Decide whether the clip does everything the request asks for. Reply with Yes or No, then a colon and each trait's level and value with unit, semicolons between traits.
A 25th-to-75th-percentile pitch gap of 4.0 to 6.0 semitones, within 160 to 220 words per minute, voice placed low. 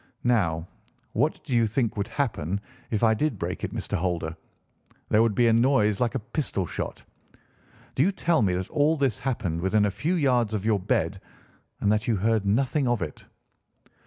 Yes: average, 4.6 semitones; average, 190 wpm; low, 110 Hz